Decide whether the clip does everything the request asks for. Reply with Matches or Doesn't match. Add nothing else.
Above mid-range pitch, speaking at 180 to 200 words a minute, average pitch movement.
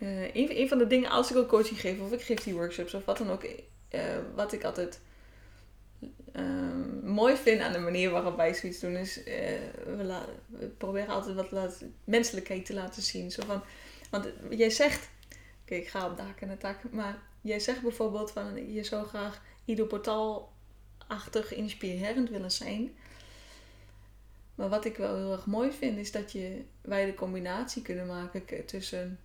Matches